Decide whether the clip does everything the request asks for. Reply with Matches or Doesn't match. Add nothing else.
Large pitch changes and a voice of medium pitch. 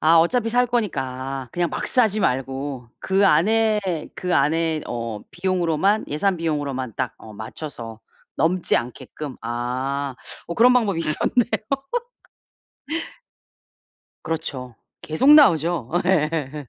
Matches